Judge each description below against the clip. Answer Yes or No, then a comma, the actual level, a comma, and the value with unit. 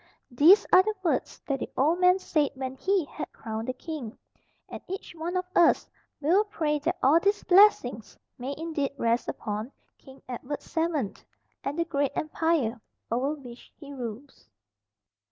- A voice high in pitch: Yes, very high, 290 Hz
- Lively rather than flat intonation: No, average, 4.8 semitones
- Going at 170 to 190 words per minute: No, average, 160 wpm